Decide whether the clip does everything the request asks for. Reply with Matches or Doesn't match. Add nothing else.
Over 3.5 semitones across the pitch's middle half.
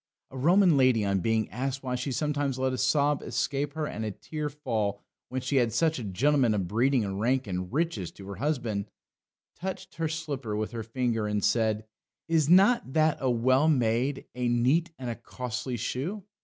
Matches